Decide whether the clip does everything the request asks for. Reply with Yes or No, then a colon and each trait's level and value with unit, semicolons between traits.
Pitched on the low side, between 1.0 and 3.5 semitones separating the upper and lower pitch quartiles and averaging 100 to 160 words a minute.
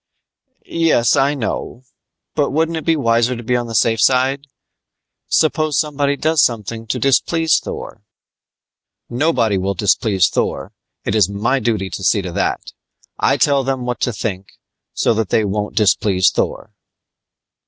No: low, 120 Hz; average, 4.9 semitones; average, 155 wpm